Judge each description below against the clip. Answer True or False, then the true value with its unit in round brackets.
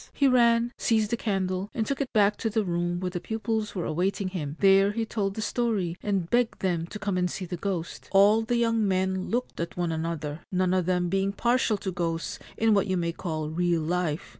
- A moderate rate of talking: False (225 wpm)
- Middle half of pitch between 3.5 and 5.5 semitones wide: True (3.9 semitones)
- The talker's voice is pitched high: True (195 Hz)